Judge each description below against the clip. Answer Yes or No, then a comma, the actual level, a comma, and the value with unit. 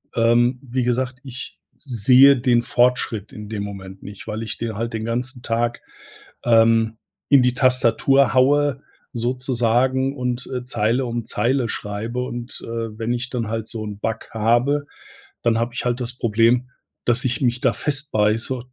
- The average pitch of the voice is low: Yes, low, 120 Hz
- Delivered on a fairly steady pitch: Yes, narrow, 2.0 semitones